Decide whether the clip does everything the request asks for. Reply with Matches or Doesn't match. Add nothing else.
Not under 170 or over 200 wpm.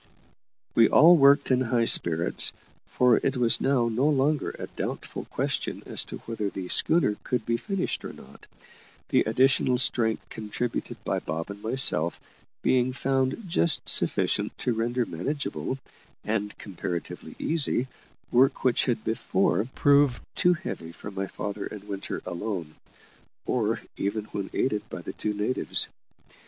Doesn't match